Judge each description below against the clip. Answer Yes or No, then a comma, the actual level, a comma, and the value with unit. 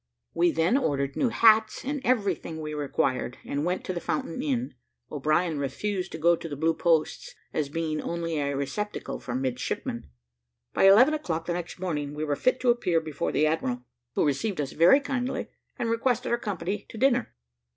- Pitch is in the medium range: Yes, medium, 170 Hz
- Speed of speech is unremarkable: Yes, average, 185 wpm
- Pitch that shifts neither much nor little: No, wide, 7.0 semitones